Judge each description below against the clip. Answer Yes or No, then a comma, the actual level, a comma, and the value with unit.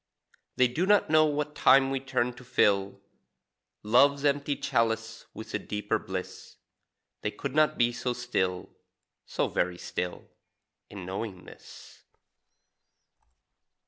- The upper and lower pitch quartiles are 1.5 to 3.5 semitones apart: No, wide, 5.6 semitones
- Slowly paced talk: Yes, slow, 125 wpm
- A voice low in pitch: Yes, low, 120 Hz